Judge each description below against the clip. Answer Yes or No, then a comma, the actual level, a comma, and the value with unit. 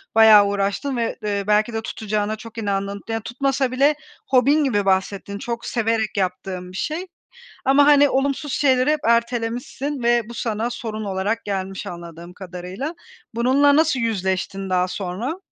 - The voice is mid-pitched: No, high, 225 Hz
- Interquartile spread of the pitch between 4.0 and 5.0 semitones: Yes, average, 4.7 semitones